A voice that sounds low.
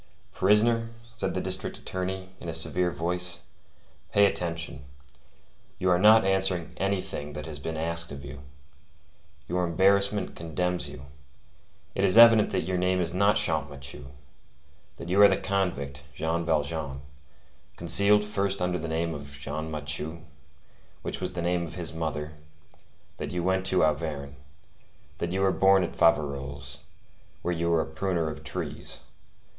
Yes: very low, 85 Hz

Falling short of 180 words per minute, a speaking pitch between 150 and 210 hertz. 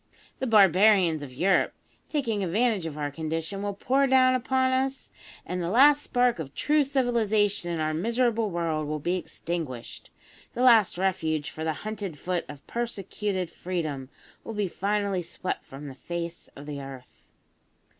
Yes: average, 160 wpm; high, 190 Hz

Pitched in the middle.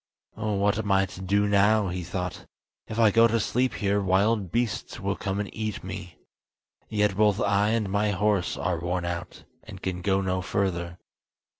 No: low, 100 Hz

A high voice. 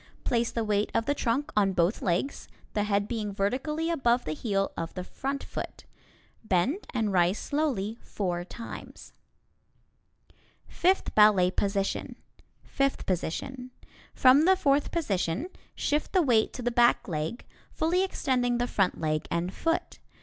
Yes: high, 230 Hz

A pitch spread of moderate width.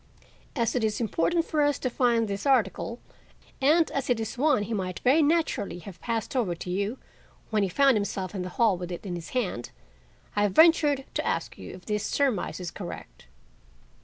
No: wide, 6.3 semitones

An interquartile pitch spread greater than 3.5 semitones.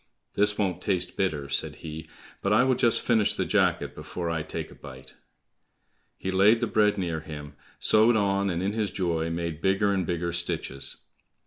Yes: average, 4.2 semitones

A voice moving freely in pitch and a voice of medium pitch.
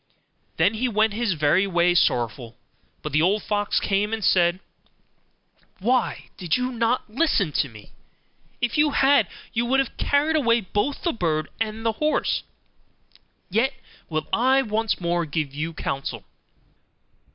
No: wide, 6.4 semitones; high, 210 Hz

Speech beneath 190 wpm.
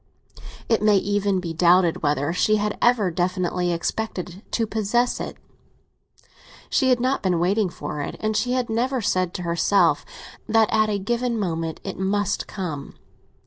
Yes: average, 160 wpm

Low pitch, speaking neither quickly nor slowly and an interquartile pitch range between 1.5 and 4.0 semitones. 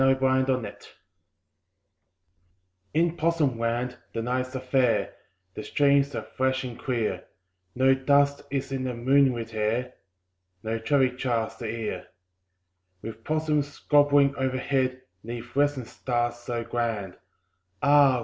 No: low, 130 Hz; slow, 125 wpm; average, 2.9 semitones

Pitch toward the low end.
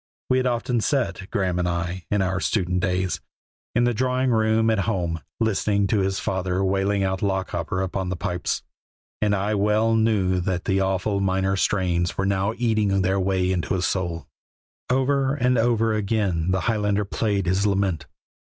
Yes: very low, 95 Hz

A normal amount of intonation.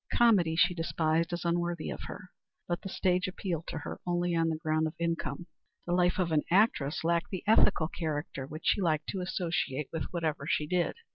No: narrow, 2.2 semitones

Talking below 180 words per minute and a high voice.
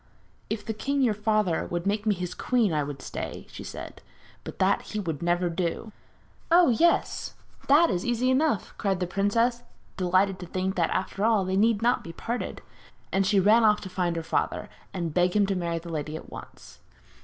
No: average, 200 wpm; high, 195 Hz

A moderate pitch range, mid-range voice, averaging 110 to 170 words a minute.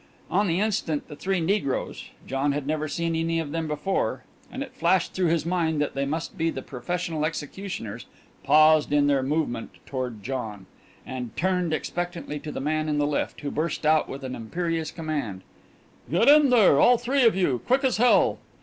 No: average, 3.7 semitones; medium, 155 Hz; average, 190 wpm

